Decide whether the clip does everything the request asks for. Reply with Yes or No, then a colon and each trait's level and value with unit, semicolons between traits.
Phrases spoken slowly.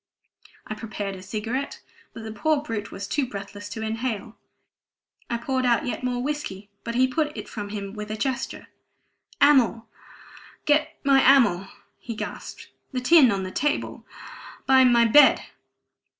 No: average, 155 wpm